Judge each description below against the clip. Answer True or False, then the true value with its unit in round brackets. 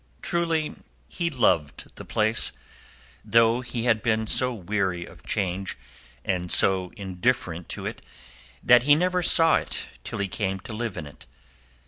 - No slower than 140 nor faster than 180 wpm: True (150 wpm)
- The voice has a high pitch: False (110 Hz)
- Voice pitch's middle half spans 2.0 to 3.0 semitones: False (5.3 semitones)